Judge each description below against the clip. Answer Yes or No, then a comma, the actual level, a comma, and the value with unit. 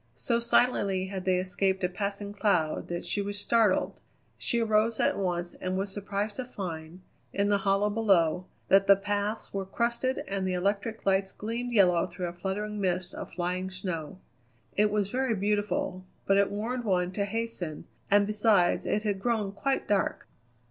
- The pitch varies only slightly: Yes, narrow, 2.3 semitones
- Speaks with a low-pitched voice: No, high, 200 Hz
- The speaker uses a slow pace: No, average, 175 wpm